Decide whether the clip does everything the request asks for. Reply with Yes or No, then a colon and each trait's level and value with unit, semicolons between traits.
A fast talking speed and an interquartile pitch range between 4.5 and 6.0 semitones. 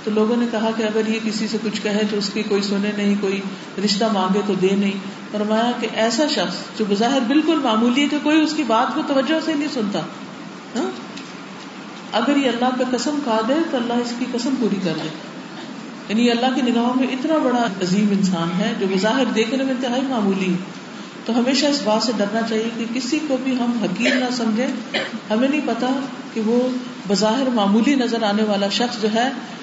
No: fast, 210 wpm; average, 3.5 semitones